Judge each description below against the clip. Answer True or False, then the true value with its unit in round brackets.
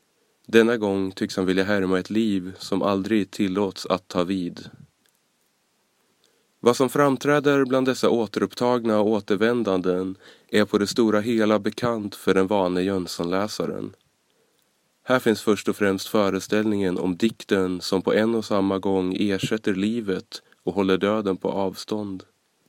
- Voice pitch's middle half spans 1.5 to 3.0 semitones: True (2.6 semitones)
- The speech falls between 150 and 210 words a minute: False (140 wpm)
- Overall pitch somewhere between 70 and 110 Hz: True (105 Hz)